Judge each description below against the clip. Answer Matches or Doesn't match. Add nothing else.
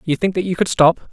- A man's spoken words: Matches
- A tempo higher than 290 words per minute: Matches